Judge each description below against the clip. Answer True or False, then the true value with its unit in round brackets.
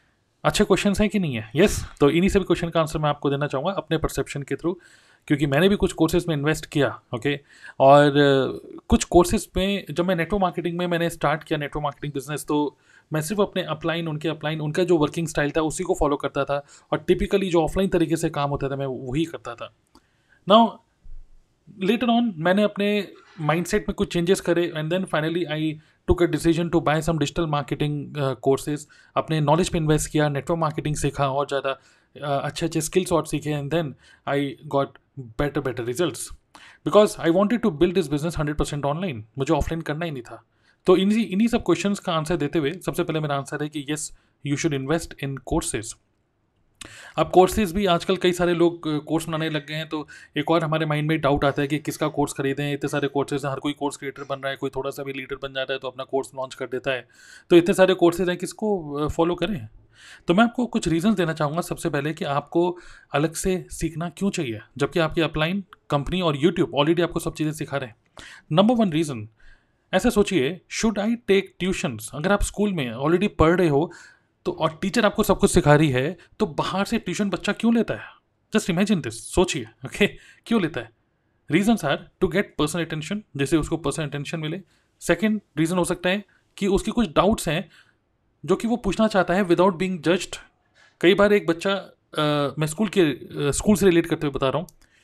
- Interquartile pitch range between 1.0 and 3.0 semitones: False (4.3 semitones)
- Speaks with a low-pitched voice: False (160 Hz)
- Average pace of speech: False (215 wpm)